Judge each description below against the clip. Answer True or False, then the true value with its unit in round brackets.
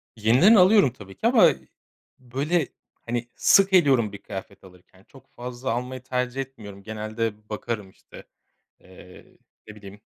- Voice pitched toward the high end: False (120 Hz)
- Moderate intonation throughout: True (4.1 semitones)